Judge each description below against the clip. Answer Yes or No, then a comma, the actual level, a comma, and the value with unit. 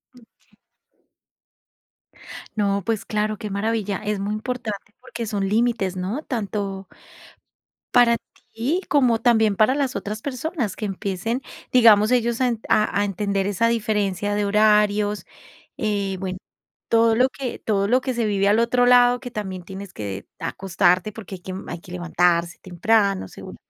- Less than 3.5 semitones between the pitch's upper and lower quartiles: Yes, average, 3.0 semitones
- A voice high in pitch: Yes, high, 210 Hz